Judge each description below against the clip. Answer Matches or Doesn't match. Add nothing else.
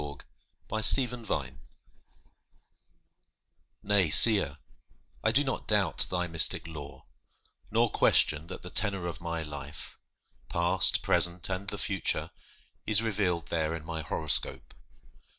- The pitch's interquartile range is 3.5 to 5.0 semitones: Matches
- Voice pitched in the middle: Doesn't match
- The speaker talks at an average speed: Doesn't match